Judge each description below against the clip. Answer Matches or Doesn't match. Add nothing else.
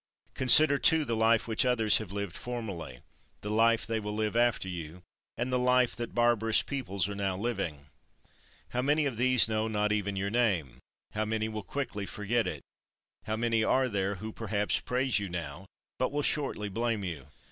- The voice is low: Matches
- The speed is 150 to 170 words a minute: Doesn't match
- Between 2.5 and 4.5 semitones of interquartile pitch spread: Matches